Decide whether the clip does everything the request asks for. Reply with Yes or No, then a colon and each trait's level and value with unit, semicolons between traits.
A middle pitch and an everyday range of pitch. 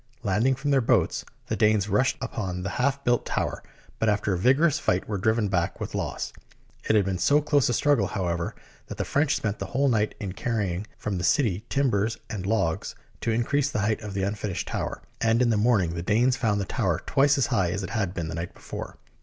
No: low, 110 Hz; average, 4.6 semitones